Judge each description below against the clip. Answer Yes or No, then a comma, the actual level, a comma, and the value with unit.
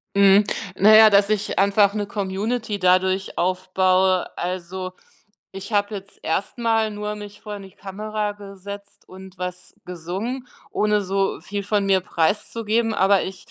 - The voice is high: Yes, high, 200 Hz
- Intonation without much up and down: Yes, narrow, 2.0 semitones